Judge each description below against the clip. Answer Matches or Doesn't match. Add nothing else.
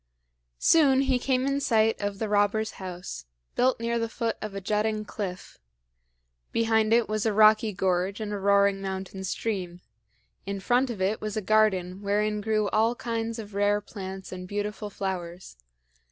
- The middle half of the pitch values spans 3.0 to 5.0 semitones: Doesn't match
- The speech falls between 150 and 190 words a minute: Matches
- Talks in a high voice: Matches